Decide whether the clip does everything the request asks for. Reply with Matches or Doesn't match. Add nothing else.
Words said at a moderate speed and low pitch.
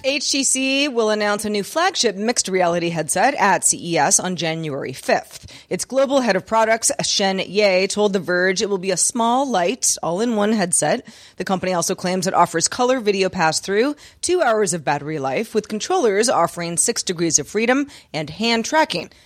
Doesn't match